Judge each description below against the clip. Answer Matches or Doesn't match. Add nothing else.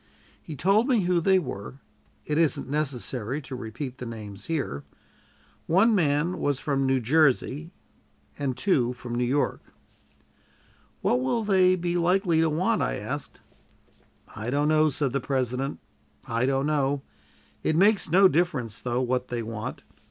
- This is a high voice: Doesn't match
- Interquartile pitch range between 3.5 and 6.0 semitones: Matches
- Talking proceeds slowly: Doesn't match